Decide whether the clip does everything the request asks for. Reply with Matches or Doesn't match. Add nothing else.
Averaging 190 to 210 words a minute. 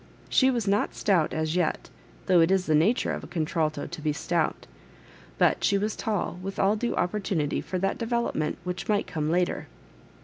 Matches